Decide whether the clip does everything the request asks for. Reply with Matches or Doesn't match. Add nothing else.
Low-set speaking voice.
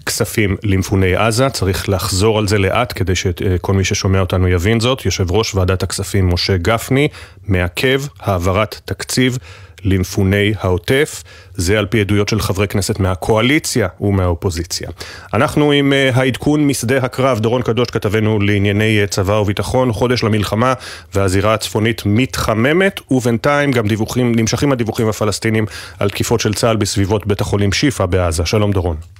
Matches